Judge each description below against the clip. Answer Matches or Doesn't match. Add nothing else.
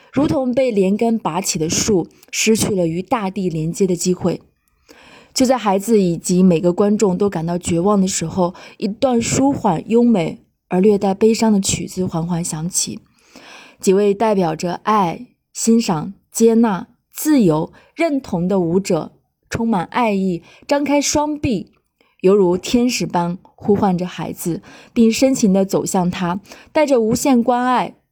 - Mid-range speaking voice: Doesn't match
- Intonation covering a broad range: Doesn't match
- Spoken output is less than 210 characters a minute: Doesn't match